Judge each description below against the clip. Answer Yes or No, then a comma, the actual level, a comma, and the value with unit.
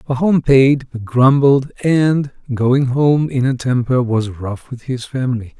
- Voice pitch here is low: Yes, low, 130 Hz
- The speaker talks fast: No, average, 160 wpm